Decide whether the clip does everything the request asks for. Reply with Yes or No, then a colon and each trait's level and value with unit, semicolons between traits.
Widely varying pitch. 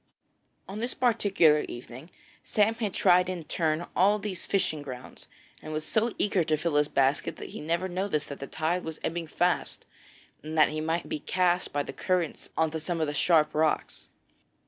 No: average, 3.3 semitones